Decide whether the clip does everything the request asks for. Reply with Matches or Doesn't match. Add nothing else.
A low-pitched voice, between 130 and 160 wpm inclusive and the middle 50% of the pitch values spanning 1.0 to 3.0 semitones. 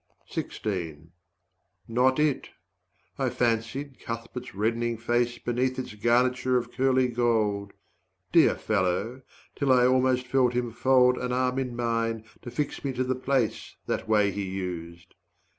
Matches